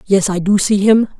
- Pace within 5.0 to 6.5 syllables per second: Yes, 5.2 syllables/s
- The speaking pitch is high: Yes, high, 200 Hz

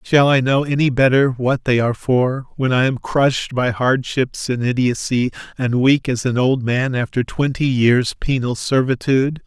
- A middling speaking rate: Yes, average, 175 wpm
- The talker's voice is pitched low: Yes, low, 130 Hz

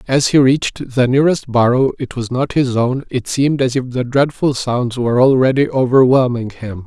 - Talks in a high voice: No, low, 130 Hz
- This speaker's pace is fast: No, average, 175 wpm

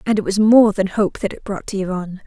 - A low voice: No, high, 200 Hz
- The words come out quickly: Yes, fast, 290 wpm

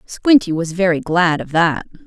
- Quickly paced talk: No, average, 175 wpm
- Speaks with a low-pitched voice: No, medium, 180 Hz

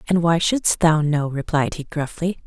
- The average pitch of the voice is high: No, medium, 160 Hz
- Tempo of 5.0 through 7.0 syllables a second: No, 4.4 syllables/s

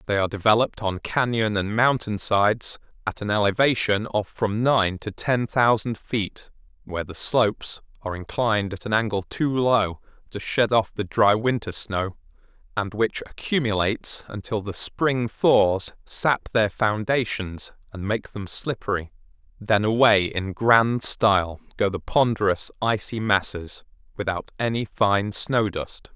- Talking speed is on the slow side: No, average, 145 wpm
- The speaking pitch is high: No, low, 105 Hz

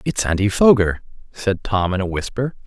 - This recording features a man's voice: Yes, male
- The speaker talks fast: No, average, 180 wpm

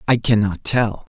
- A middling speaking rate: Yes, average, 155 wpm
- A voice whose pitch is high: No, low, 110 Hz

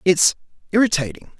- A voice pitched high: No, medium, 175 Hz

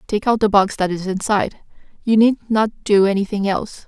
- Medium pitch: No, high, 205 Hz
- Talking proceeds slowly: No, average, 200 wpm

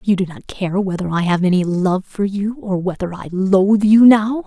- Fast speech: Yes, fast, 230 wpm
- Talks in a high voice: Yes, high, 195 Hz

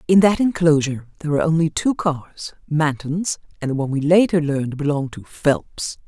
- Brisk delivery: No, average, 160 wpm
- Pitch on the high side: No, medium, 155 Hz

